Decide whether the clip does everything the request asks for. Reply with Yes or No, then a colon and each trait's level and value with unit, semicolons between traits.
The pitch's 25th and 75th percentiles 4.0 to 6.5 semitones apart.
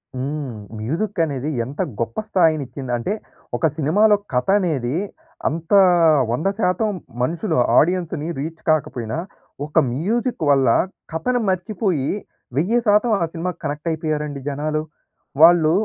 Yes: average, 4.4 semitones